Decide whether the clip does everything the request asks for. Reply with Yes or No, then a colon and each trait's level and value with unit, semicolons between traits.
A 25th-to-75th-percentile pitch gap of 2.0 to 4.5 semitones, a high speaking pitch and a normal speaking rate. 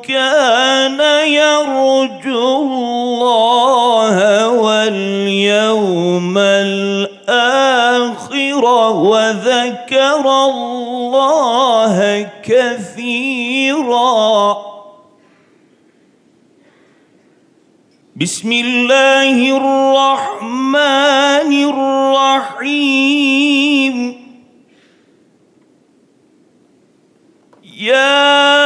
No: average, 3.3 semitones; very high, 255 Hz; slow, 25 wpm